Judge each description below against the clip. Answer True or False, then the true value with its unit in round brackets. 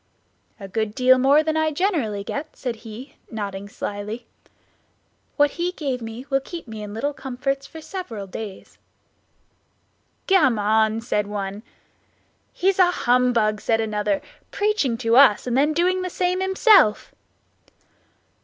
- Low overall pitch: False (250 Hz)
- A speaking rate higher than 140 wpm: False (135 wpm)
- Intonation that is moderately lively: False (6.5 semitones)